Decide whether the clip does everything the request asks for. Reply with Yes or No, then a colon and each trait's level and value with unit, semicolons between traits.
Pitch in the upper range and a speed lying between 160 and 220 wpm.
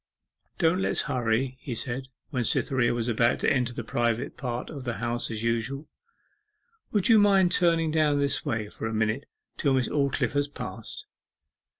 No: low, 130 Hz; average, 175 wpm